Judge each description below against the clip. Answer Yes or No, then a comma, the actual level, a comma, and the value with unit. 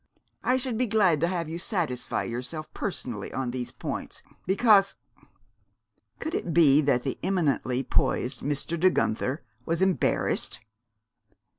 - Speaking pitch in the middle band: Yes, medium, 160 Hz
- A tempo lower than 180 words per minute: Yes, average, 140 wpm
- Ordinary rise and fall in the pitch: No, wide, 6.6 semitones